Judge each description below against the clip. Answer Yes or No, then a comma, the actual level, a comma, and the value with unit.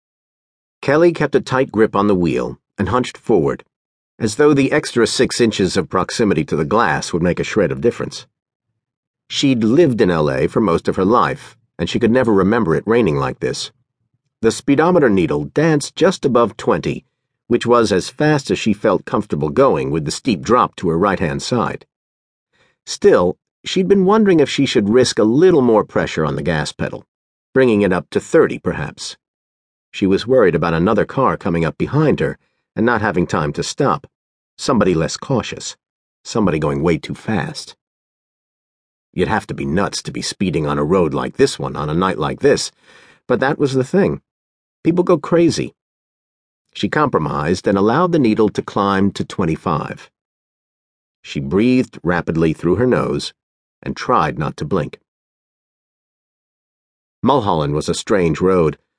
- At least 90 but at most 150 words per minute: No, average, 175 wpm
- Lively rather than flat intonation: Yes, wide, 8.8 semitones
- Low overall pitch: Yes, low, 120 Hz